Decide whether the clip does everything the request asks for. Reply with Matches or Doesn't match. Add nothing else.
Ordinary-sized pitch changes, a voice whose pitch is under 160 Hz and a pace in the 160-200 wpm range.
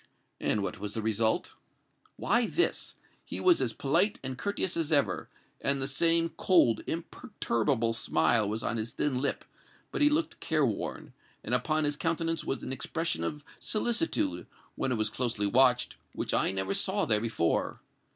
Doesn't match